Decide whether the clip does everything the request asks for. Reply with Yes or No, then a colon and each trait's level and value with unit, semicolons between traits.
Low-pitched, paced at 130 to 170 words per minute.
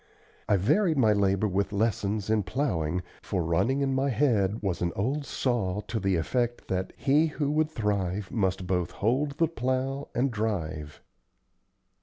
Yes: low, 110 Hz; average, 160 wpm